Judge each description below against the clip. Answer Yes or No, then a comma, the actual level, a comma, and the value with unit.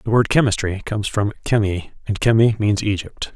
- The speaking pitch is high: No, low, 105 Hz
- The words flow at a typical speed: Yes, average, 180 wpm